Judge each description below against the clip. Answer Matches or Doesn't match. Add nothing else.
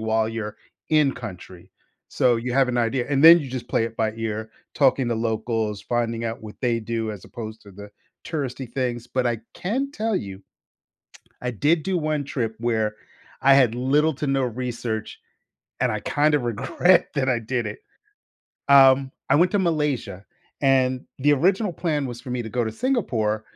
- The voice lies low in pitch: Matches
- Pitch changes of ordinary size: Matches